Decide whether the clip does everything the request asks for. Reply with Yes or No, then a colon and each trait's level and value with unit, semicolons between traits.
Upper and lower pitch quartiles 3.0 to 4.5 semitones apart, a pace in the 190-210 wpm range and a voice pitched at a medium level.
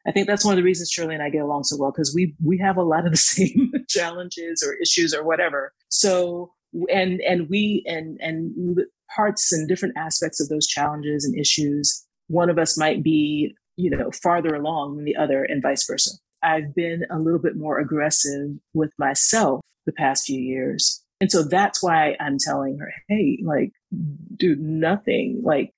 Yes: average, 3.6 semitones; average, 195 wpm; medium, 165 Hz